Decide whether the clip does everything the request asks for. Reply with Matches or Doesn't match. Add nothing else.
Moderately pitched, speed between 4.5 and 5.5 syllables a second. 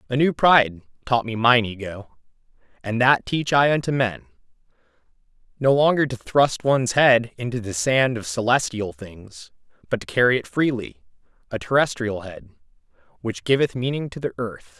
Doesn't match